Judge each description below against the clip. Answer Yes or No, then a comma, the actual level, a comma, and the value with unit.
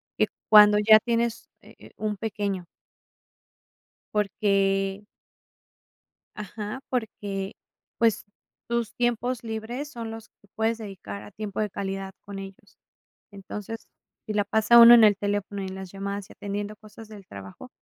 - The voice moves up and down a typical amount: No, narrow, 2.2 semitones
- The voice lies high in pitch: Yes, high, 210 Hz